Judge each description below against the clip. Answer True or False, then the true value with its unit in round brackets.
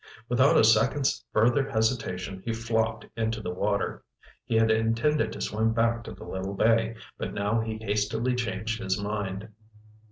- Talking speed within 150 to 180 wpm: True (160 wpm)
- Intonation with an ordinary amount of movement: False (1.8 semitones)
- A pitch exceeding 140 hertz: False (110 Hz)